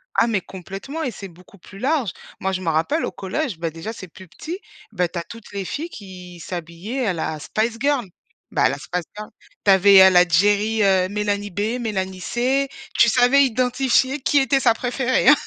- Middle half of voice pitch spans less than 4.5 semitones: No, average, 5.3 semitones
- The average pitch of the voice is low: No, high, 205 Hz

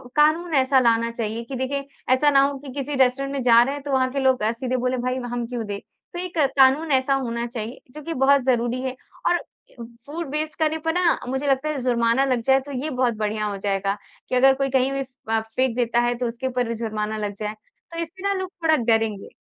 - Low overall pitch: No, very high, 255 Hz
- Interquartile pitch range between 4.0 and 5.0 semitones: No, average, 3.2 semitones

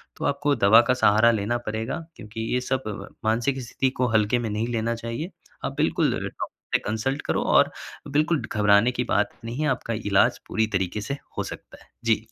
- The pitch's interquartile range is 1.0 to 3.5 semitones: Yes, average, 3.0 semitones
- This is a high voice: No, low, 115 Hz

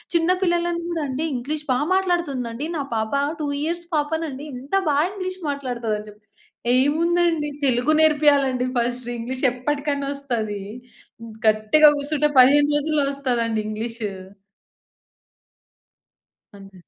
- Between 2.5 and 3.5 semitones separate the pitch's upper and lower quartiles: No, average, 4.2 semitones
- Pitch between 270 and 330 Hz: Yes, very high, 280 Hz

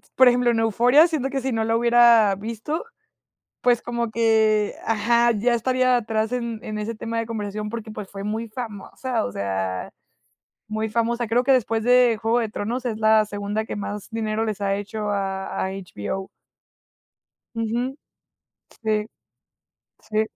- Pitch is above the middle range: Yes, high, 225 Hz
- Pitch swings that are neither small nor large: No, narrow, 2.2 semitones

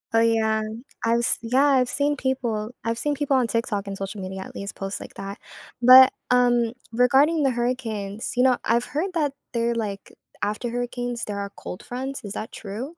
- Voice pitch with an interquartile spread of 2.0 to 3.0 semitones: No, average, 3.4 semitones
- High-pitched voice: Yes, high, 235 Hz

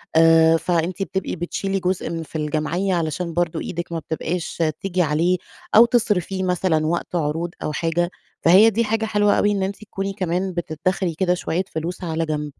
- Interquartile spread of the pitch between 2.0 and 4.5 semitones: Yes, average, 2.8 semitones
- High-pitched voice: No, medium, 175 Hz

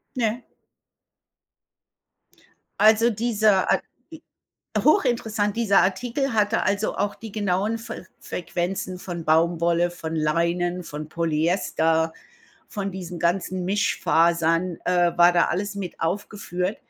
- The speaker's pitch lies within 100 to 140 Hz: No, medium, 185 Hz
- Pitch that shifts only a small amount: No, average, 3.6 semitones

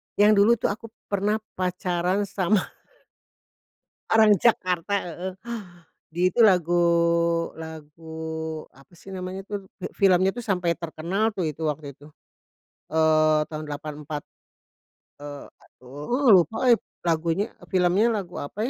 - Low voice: No, medium, 175 Hz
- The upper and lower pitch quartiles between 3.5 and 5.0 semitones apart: Yes, average, 4.2 semitones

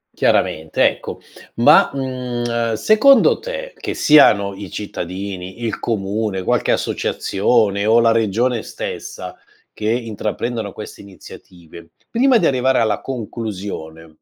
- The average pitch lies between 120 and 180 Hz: No, low, 110 Hz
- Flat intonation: No, average, 4.1 semitones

